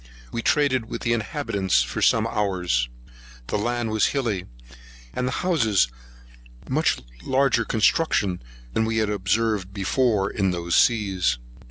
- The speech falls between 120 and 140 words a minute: Yes, slow, 135 wpm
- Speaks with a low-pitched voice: Yes, low, 105 Hz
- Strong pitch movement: No, average, 3.8 semitones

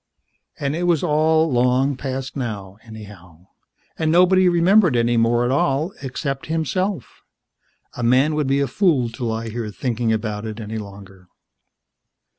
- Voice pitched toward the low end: Yes, low, 130 Hz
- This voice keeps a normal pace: Yes, average, 150 wpm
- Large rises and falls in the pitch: Yes, wide, 5.8 semitones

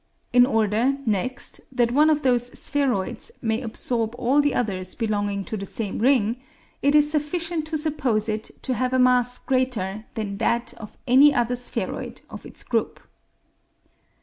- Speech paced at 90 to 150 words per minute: No, average, 160 wpm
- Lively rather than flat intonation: No, average, 4.0 semitones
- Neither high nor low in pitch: No, high, 245 Hz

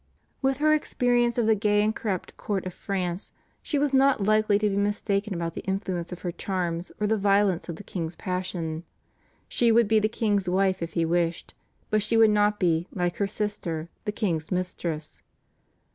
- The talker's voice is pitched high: Yes, high, 200 Hz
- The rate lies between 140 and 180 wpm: No, average, 190 wpm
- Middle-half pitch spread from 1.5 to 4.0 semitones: Yes, average, 3.4 semitones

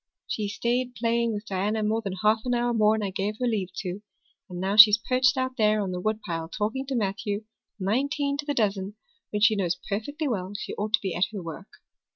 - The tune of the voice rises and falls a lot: No, average, 3.3 semitones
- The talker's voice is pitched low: No, high, 215 Hz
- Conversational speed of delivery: No, fast, 220 wpm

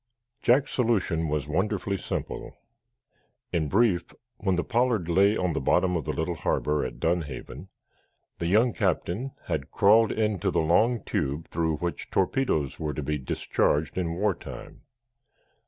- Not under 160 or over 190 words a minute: No, average, 150 wpm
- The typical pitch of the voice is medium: No, very low, 90 Hz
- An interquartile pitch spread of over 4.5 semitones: Yes, average, 5.1 semitones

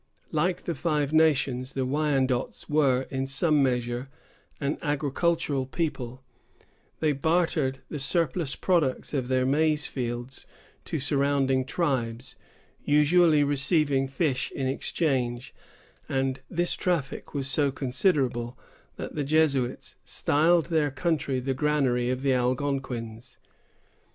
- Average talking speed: No, slow, 115 wpm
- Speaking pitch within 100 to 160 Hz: Yes, medium, 140 Hz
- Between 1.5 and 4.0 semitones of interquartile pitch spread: Yes, average, 2.9 semitones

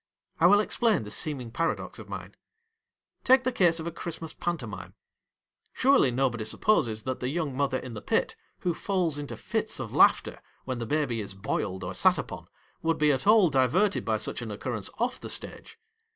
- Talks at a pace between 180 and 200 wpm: Yes, average, 190 wpm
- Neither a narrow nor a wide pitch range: No, wide, 6.6 semitones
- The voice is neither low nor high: Yes, medium, 145 Hz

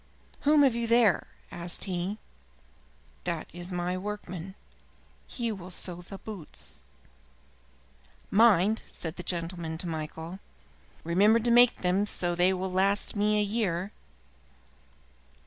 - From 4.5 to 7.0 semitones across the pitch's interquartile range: No, average, 3.2 semitones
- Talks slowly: Yes, slow, 130 wpm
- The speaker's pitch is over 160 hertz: Yes, medium, 185 Hz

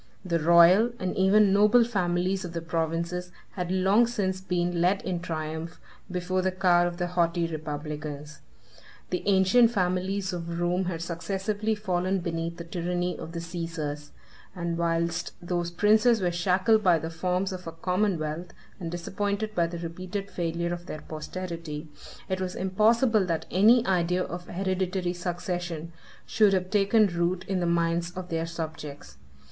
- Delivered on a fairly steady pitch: Yes, narrow, 2.1 semitones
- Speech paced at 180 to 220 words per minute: No, average, 160 wpm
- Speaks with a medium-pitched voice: Yes, medium, 175 Hz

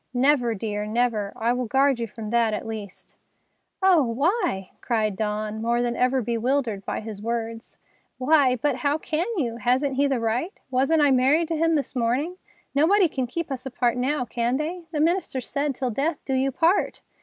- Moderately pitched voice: No, very high, 255 Hz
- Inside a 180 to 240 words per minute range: Yes, average, 185 wpm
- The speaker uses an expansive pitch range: No, average, 4.3 semitones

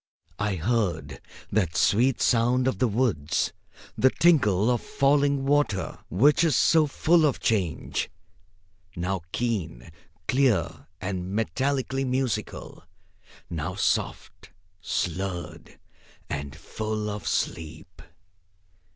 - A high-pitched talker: No, low, 110 Hz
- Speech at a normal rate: No, slow, 100 wpm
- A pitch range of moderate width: No, wide, 6.9 semitones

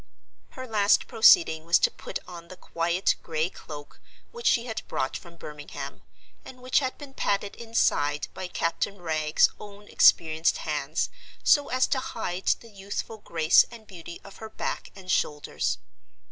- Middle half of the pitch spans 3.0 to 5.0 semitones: No, wide, 5.4 semitones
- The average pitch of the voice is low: No, medium, 185 Hz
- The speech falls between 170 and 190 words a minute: No, average, 160 wpm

